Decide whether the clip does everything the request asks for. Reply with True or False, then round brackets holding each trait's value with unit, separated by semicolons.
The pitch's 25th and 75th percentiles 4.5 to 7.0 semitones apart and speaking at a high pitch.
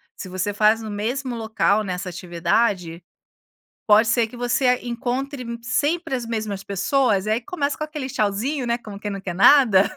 False (4.1 semitones; 225 Hz)